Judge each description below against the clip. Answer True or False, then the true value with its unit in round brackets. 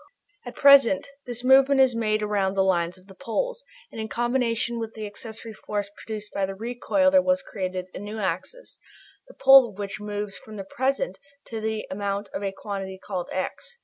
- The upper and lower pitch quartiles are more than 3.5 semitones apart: True (4.2 semitones)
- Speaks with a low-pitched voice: False (215 Hz)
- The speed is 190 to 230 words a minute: True (195 wpm)